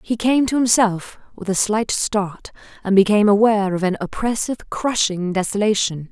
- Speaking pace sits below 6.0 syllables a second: Yes, 5.2 syllables/s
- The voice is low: No, high, 210 Hz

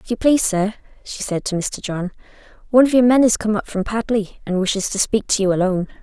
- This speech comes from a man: No, female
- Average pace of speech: No, fast, 250 wpm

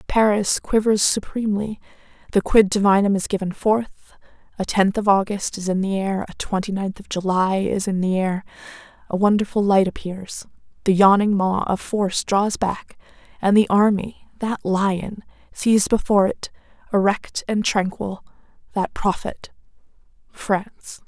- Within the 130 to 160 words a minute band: Yes, average, 145 wpm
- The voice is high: Yes, high, 200 Hz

